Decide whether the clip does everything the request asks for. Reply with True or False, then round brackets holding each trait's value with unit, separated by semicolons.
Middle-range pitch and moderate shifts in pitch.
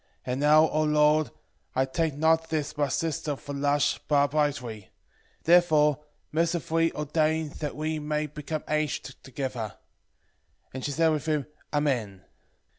False (150 Hz; 1.8 semitones)